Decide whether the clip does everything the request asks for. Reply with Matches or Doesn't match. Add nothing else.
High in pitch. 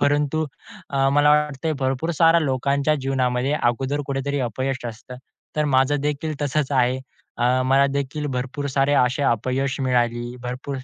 Doesn't match